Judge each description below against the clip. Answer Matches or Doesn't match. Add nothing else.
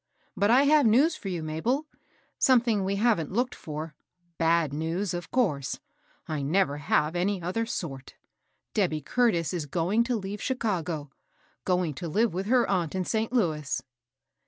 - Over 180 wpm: Doesn't match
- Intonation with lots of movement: Matches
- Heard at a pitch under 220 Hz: Matches